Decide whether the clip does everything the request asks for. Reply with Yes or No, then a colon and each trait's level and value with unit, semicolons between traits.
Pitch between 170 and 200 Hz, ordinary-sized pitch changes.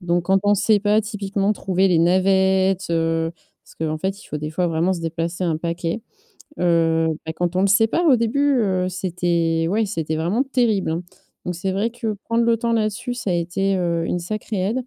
Yes: high, 190 Hz; average, 4.0 semitones